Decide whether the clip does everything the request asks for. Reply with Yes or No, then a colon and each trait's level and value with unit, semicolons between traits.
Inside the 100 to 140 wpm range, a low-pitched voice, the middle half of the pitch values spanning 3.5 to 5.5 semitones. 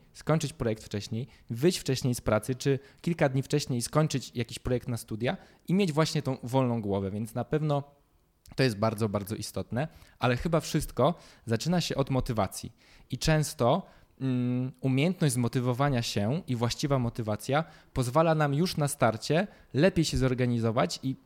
No: average, 150 wpm; low, 130 Hz; average, 4.3 semitones